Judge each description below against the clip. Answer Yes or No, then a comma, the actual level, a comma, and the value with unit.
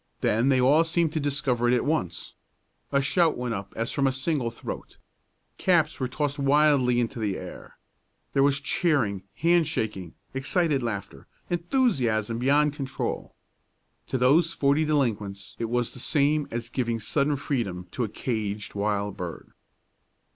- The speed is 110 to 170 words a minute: Yes, average, 155 wpm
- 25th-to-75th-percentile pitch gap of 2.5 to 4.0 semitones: No, average, 4.9 semitones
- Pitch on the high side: No, low, 130 Hz